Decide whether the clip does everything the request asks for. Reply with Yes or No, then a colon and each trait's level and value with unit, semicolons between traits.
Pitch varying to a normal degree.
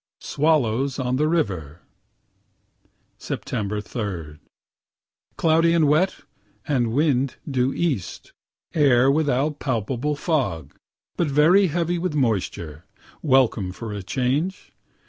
No: wide, 5.9 semitones